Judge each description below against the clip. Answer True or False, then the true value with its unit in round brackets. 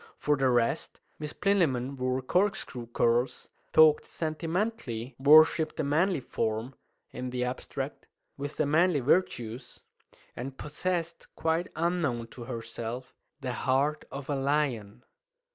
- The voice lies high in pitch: False (135 Hz)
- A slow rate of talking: True (125 wpm)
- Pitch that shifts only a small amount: False (4.3 semitones)